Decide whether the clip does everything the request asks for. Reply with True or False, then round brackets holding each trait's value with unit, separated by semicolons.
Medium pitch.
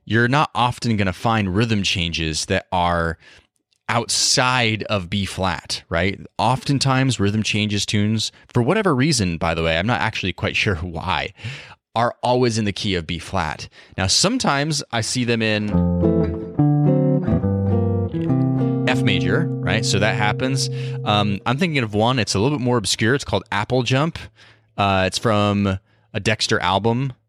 False (110 Hz)